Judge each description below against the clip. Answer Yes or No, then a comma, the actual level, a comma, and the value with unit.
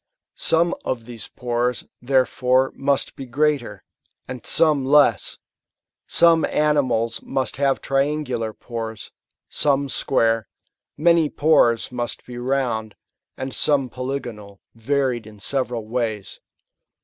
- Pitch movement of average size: Yes, average, 3.4 semitones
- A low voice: Yes, low, 130 Hz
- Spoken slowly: Yes, slow, 110 wpm